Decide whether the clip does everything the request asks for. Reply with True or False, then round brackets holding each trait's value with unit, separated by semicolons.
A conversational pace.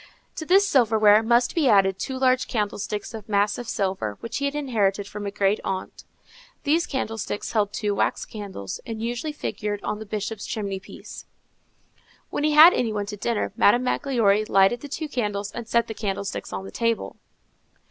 True (180 wpm)